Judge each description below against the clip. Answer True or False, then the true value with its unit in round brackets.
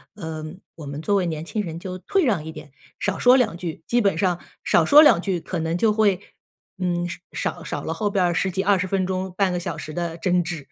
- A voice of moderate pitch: True (180 Hz)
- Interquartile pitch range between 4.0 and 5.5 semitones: False (3.3 semitones)